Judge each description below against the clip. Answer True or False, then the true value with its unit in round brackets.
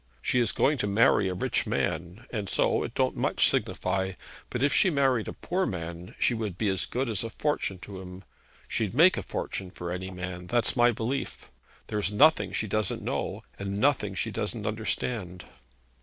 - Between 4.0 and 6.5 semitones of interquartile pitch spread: True (4.5 semitones)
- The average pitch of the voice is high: False (105 Hz)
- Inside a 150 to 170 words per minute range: False (195 wpm)